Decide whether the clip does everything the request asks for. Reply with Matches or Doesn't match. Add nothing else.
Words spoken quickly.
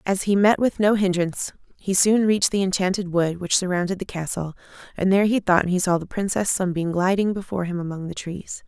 Matches